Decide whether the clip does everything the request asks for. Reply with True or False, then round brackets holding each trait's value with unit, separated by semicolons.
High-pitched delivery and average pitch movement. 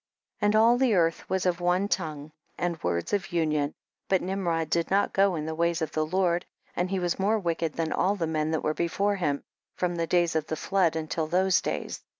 False (170 Hz; 3.0 semitones)